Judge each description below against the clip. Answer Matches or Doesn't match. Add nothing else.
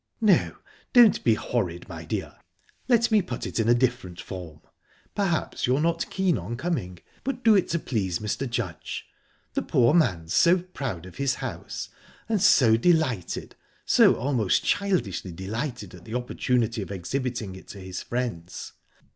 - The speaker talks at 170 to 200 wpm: Doesn't match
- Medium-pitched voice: Doesn't match